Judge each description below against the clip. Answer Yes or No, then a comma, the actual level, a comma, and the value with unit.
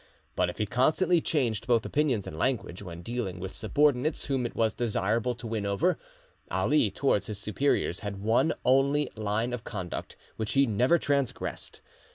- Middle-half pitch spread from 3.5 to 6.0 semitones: Yes, average, 4.9 semitones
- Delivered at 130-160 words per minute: No, average, 170 wpm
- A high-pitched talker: No, low, 115 Hz